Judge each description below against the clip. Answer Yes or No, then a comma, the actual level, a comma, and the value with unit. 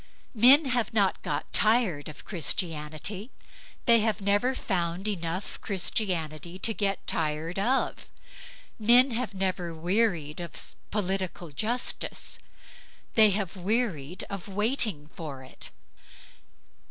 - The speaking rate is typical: No, slow, 110 wpm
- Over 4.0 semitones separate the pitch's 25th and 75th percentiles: Yes, average, 4.7 semitones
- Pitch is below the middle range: No, high, 195 Hz